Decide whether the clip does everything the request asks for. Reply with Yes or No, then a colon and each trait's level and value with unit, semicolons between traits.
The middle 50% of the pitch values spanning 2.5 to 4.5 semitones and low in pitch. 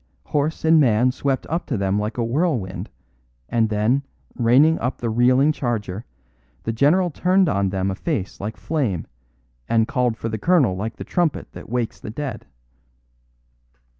No: wide, 5.5 semitones; low, 120 Hz